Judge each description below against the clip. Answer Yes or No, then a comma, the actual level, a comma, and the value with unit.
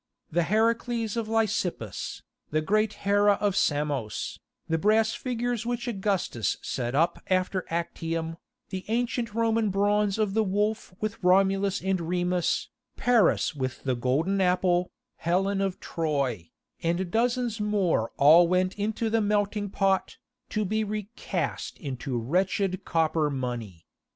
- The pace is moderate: No, slow, 130 wpm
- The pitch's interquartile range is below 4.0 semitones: No, average, 4.6 semitones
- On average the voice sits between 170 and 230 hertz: Yes, high, 190 Hz